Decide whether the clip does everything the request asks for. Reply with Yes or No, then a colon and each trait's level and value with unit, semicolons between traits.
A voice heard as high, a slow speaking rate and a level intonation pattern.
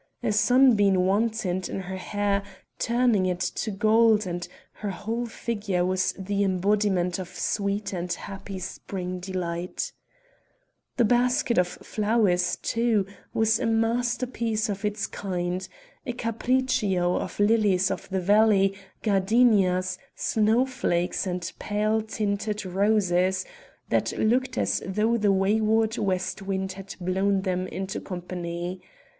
No: high, 200 Hz; slow, 125 wpm; average, 3.1 semitones